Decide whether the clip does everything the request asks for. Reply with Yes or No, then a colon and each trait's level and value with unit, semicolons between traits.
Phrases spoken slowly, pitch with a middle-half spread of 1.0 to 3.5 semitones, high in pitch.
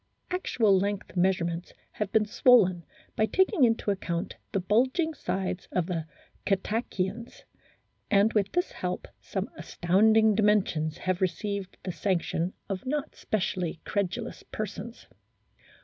Yes: slow, 130 wpm; average, 3.2 semitones; high, 200 Hz